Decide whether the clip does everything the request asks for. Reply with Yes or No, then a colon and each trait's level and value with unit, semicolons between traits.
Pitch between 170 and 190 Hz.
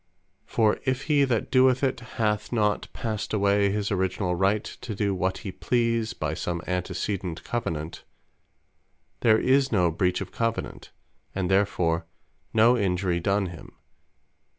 No: low, 100 Hz